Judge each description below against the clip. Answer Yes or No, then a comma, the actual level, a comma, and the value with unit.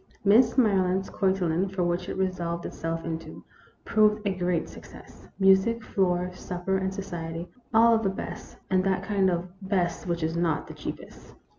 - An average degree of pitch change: No, narrow, 2.0 semitones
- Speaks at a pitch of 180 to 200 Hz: Yes, medium, 185 Hz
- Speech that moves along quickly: No, average, 170 wpm